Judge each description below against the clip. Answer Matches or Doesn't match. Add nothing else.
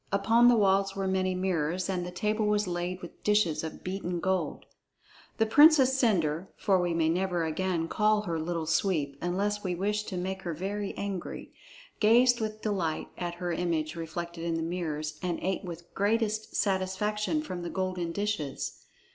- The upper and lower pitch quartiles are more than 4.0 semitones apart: Doesn't match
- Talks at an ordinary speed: Matches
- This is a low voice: Doesn't match